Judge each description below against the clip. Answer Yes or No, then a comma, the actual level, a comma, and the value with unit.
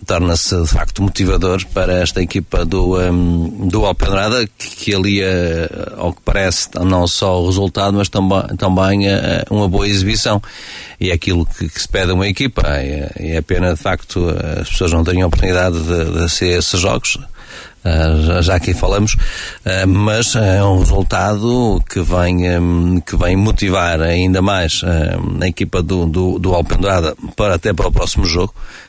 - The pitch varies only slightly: Yes, narrow, 2.2 semitones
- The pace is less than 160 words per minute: No, average, 165 wpm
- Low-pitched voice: Yes, very low, 90 Hz